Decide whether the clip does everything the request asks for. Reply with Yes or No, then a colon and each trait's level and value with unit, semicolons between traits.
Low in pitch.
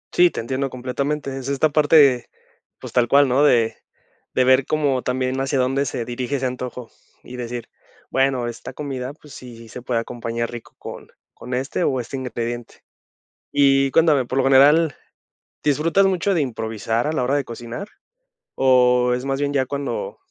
Yes: low, 130 Hz